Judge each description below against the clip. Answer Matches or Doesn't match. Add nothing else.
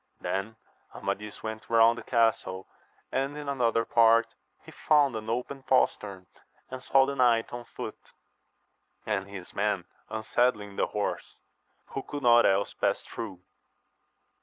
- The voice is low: Matches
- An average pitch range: Matches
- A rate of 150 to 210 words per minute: Doesn't match